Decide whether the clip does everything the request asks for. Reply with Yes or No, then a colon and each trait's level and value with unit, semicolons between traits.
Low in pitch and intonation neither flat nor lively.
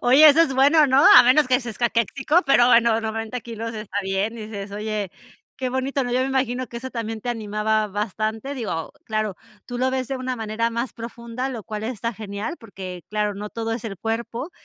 No: high, 230 Hz; average, 3.1 semitones